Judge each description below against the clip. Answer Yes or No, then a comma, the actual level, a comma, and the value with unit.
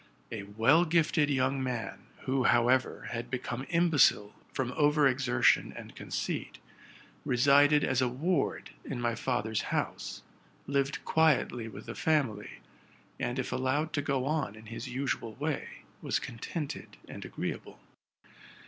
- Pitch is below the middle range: Yes, low, 130 Hz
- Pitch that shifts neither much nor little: Yes, average, 3.4 semitones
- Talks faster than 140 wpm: No, slow, 135 wpm